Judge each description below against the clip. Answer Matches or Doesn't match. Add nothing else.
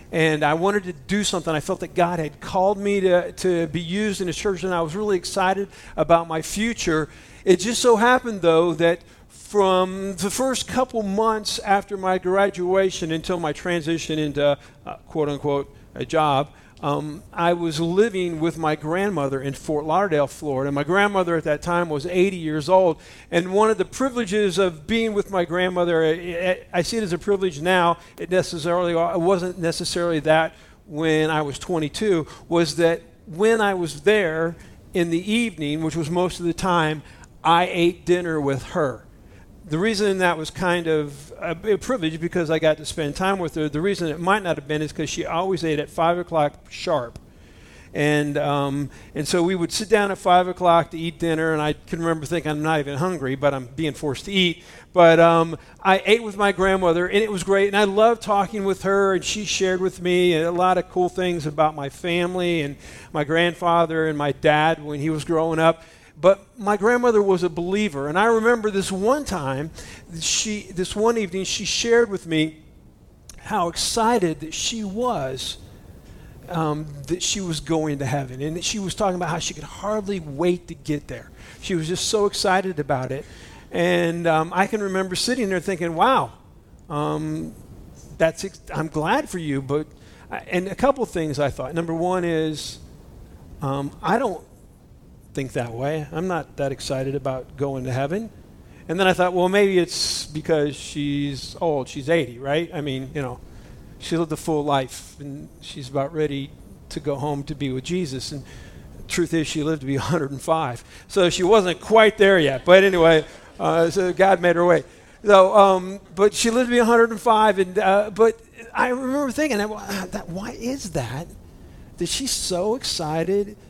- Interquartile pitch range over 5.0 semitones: Doesn't match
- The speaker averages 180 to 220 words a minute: Matches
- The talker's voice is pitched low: Doesn't match